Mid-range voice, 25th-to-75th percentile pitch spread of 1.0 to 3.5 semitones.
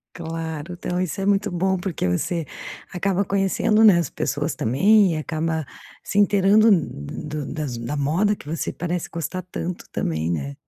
No: medium, 170 Hz; average, 4.3 semitones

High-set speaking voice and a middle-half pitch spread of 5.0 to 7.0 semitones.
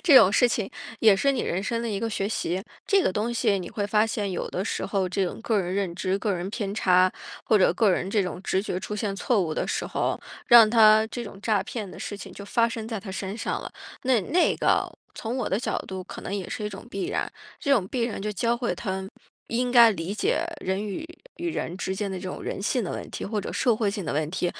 No: high, 205 Hz; average, 3.3 semitones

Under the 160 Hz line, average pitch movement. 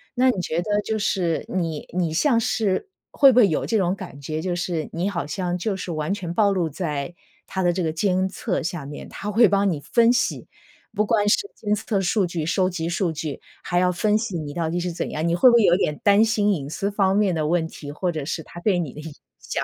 No: medium, 180 Hz; average, 4.0 semitones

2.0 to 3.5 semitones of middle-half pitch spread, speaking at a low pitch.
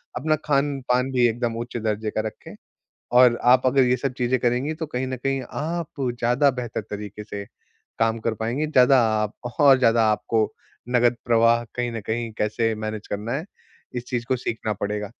Yes: narrow, 2.6 semitones; low, 120 Hz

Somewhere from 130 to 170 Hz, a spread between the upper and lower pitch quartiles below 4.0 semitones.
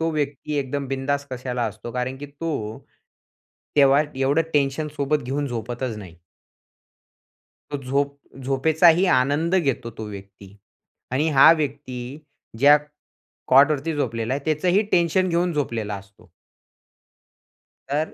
Yes: medium, 140 Hz; average, 3.3 semitones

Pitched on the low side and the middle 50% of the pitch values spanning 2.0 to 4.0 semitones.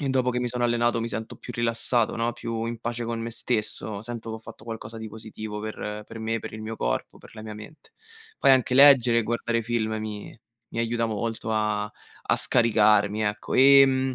No: low, 115 Hz; narrow, 1.6 semitones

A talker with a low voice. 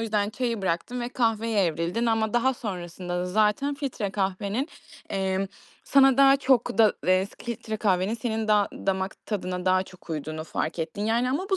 No: high, 210 Hz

